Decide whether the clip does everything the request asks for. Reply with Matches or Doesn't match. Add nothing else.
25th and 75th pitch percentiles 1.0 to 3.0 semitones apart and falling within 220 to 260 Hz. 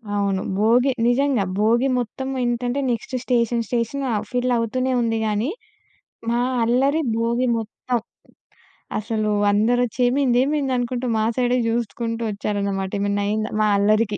Matches